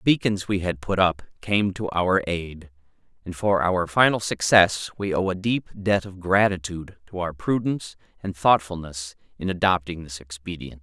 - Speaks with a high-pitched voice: No, very low, 90 Hz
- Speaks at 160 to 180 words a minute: Yes, average, 170 wpm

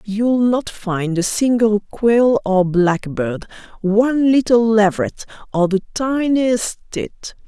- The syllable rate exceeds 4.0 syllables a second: No, 3.5 syllables/s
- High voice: Yes, high, 215 Hz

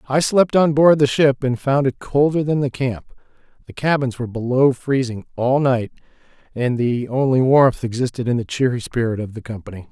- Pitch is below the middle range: Yes, low, 130 Hz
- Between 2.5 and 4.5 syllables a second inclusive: No, 5.2 syllables/s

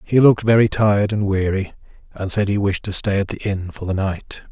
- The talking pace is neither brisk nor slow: No, fast, 240 wpm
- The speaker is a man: Yes, male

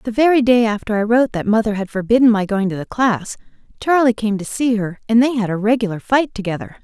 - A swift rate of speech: Yes, fast, 235 wpm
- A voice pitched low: No, high, 225 Hz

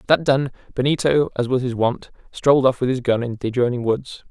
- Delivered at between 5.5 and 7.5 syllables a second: Yes, 6.0 syllables/s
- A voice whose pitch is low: Yes, low, 130 Hz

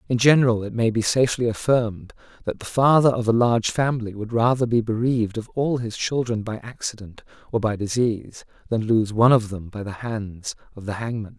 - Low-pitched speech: Yes, low, 115 Hz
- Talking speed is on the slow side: No, average, 200 wpm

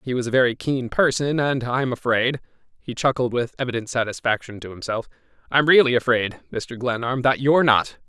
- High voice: No, low, 125 Hz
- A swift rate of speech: No, average, 165 wpm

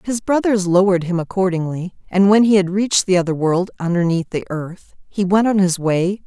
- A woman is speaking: Yes, female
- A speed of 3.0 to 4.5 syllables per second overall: No, 5.4 syllables/s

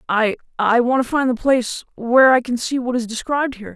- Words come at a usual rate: No, fast, 210 wpm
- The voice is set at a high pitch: Yes, high, 245 Hz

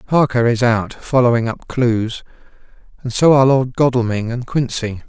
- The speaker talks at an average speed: Yes, average, 155 wpm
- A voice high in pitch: No, low, 120 Hz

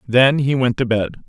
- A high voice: No, low, 125 Hz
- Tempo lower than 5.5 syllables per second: Yes, 4.8 syllables/s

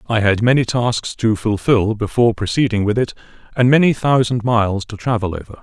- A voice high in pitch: No, low, 115 Hz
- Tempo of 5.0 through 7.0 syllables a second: Yes, 5.6 syllables/s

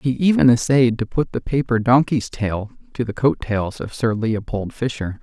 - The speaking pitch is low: Yes, low, 120 Hz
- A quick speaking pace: No, average, 195 wpm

